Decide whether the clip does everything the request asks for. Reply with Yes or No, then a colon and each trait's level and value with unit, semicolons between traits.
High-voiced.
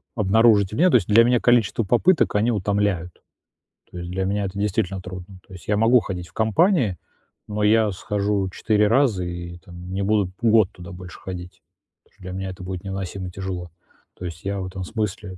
No: low, 100 Hz